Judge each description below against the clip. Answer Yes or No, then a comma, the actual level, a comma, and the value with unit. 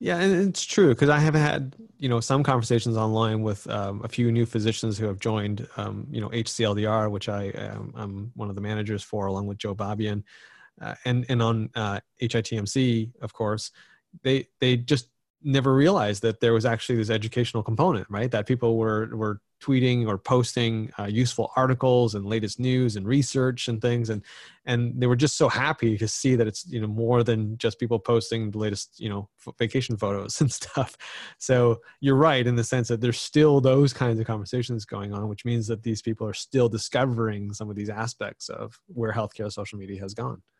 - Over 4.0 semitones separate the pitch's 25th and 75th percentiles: No, average, 2.7 semitones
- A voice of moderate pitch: No, low, 115 Hz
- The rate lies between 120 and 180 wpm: No, fast, 205 wpm